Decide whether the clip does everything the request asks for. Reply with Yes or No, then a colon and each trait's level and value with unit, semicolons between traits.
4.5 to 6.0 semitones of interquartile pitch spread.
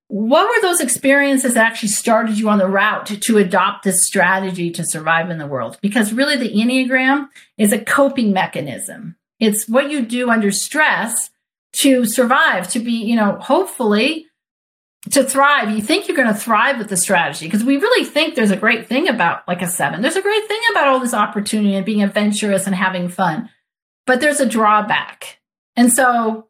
Yes: average, 5.2 semitones